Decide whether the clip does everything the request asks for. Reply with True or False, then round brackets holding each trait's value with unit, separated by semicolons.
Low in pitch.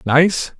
False (155 Hz)